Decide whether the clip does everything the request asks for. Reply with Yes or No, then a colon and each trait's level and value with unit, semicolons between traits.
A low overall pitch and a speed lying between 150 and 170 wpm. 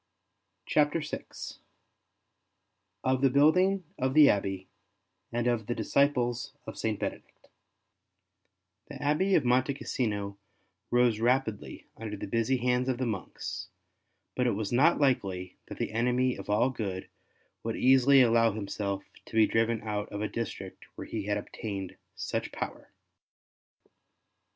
No: low, 120 Hz; average, 140 wpm